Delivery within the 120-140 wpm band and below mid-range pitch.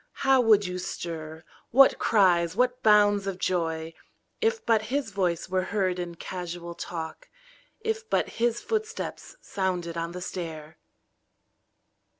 No: slow, 135 wpm; medium, 185 Hz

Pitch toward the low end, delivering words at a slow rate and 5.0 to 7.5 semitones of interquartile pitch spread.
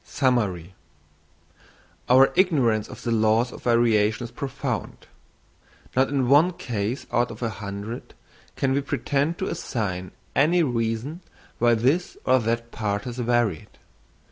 No: low, 120 Hz; slow, 130 wpm; average, 3.7 semitones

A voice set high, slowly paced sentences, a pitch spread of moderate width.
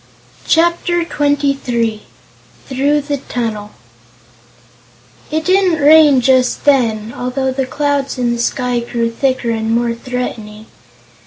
Yes: very high, 260 Hz; slow, 115 wpm; average, 3.6 semitones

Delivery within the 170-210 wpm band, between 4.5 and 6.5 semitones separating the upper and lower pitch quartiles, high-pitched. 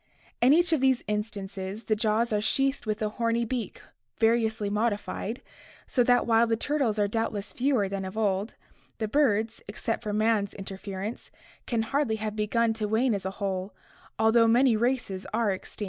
No: average, 175 wpm; narrow, 2.4 semitones; high, 220 Hz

